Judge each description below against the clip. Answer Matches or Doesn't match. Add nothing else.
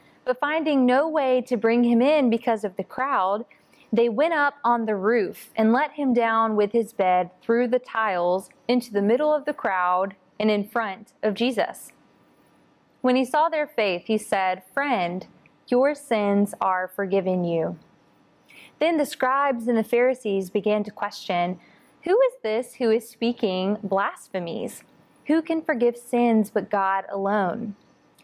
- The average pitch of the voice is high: Matches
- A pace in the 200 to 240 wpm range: Doesn't match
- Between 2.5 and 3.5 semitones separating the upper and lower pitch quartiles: Doesn't match